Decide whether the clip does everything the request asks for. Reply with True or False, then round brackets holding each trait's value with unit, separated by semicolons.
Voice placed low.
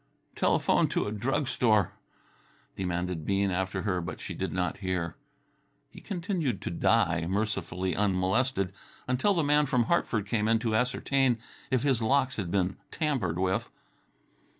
True (105 Hz)